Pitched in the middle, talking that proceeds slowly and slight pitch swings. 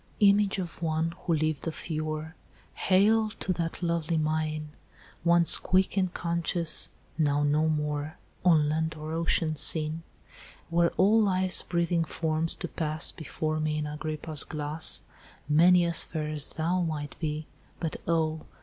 No: medium, 160 Hz; average, 145 wpm; narrow, 1.9 semitones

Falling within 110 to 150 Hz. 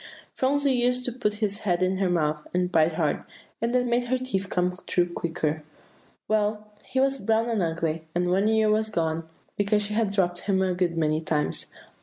No: high, 195 Hz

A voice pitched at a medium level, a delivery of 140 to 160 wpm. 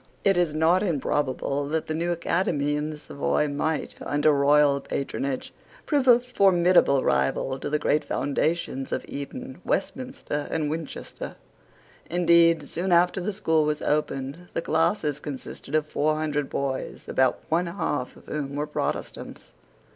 Yes: medium, 155 Hz; average, 145 wpm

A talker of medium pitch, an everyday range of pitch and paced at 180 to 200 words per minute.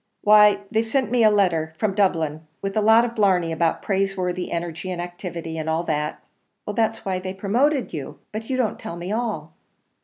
No: high, 195 Hz; average, 4.3 semitones; average, 195 wpm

